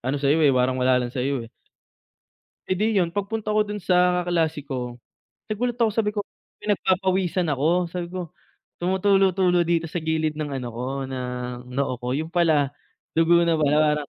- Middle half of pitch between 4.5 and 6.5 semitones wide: Yes, average, 5.2 semitones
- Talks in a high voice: No, medium, 165 Hz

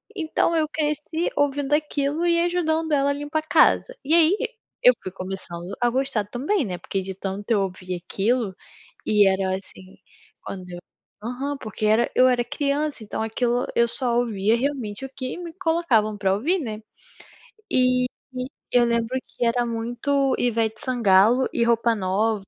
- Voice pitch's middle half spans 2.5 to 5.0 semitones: No, wide, 5.4 semitones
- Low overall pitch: No, high, 245 Hz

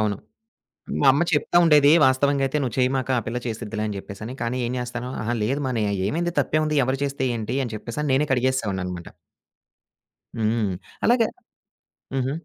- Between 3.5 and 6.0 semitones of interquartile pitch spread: Yes, average, 4.1 semitones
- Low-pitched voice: Yes, low, 125 Hz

